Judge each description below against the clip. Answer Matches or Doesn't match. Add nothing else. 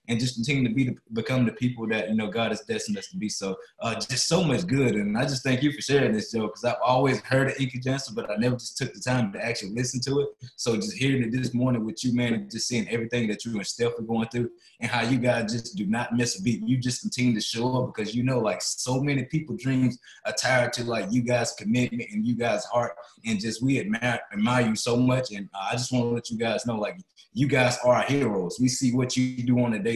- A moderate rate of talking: Doesn't match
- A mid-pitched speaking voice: Doesn't match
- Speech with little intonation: Matches